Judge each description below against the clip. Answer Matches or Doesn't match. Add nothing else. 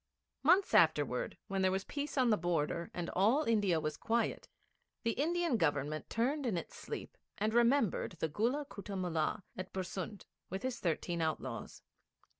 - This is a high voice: Matches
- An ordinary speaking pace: Matches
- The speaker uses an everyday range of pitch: Doesn't match